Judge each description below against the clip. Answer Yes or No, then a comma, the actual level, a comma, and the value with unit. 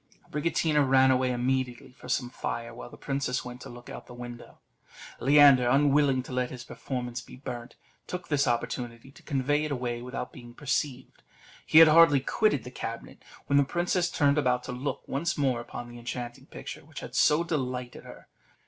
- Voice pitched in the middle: No, low, 130 Hz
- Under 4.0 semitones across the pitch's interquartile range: Yes, average, 2.8 semitones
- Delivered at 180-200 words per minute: Yes, average, 190 wpm